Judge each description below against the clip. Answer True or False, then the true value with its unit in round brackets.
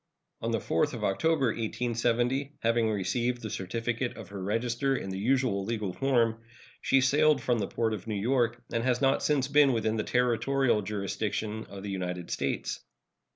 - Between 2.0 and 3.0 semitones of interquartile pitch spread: False (3.5 semitones)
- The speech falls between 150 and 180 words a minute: True (175 wpm)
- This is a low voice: True (115 Hz)